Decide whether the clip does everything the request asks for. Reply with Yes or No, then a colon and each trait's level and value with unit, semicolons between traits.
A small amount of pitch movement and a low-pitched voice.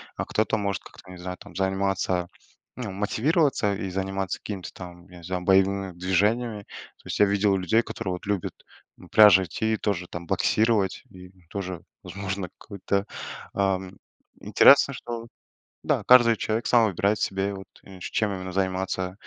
Yes: narrow, 2.3 semitones; very low, 95 Hz